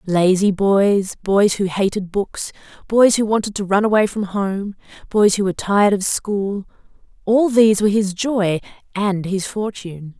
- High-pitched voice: Yes, high, 200 Hz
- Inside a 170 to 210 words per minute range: No, average, 160 wpm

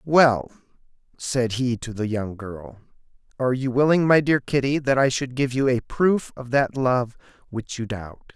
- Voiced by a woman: No, male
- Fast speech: No, average, 185 wpm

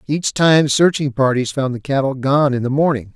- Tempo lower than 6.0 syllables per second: Yes, 5.0 syllables/s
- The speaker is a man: Yes, male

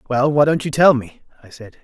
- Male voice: Yes, male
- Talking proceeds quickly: Yes, fast, 260 wpm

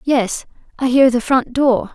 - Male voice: No, female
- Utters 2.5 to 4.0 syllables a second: Yes, 3.9 syllables/s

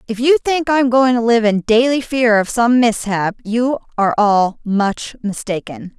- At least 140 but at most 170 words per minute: No, average, 180 wpm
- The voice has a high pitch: Yes, high, 230 Hz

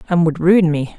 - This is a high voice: No, medium, 170 Hz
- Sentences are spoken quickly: Yes, fast, 245 wpm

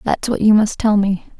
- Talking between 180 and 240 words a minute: No, fast, 260 wpm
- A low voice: No, high, 210 Hz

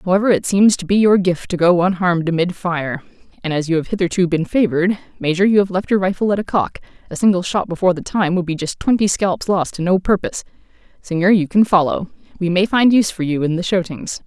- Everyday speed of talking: No, fast, 225 wpm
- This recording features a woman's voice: Yes, female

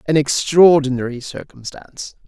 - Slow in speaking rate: Yes, slow, 80 wpm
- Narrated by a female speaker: No, male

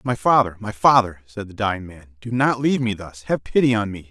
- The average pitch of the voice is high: No, low, 110 Hz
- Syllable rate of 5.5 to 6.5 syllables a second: Yes, 5.9 syllables/s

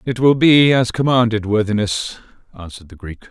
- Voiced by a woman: No, male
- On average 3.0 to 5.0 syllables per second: No, 5.6 syllables/s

